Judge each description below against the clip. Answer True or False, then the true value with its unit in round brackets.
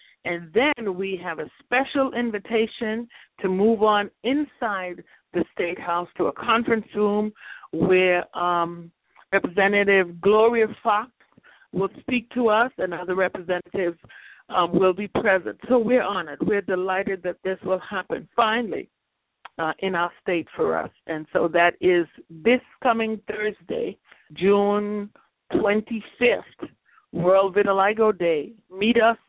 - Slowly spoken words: True (130 wpm)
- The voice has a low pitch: False (200 Hz)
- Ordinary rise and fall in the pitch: True (3.6 semitones)